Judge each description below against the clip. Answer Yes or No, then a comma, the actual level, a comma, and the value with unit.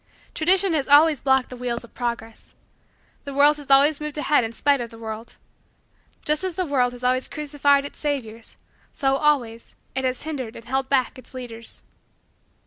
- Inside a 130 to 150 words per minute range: No, average, 180 wpm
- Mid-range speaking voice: No, very high, 270 Hz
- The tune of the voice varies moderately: Yes, average, 3.5 semitones